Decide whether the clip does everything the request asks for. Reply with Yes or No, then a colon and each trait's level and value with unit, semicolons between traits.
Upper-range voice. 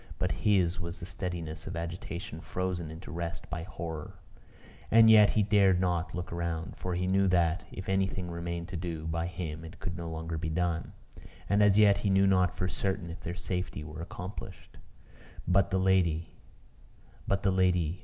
No: very low, 90 Hz